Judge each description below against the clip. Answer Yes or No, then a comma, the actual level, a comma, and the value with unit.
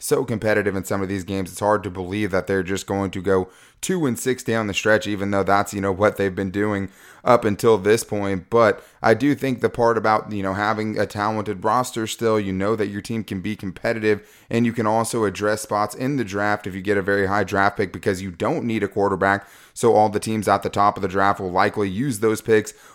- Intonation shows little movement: Yes, narrow, 2.0 semitones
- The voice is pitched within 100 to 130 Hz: Yes, low, 105 Hz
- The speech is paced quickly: Yes, fast, 250 wpm